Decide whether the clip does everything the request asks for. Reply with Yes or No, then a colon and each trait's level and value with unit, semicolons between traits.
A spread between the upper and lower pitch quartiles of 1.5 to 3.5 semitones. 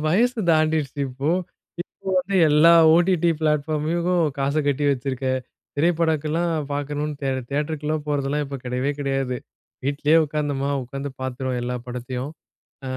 Yes: narrow, 2.6 semitones